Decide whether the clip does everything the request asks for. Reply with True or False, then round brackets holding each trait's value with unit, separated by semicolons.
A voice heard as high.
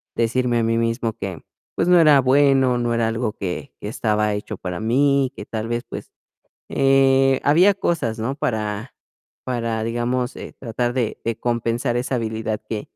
False (120 Hz)